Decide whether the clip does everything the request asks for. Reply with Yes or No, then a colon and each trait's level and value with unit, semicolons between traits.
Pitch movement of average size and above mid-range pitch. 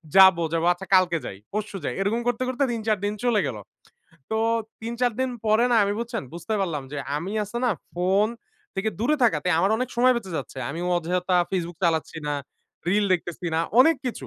Yes: average, 4.9 semitones; high, 200 Hz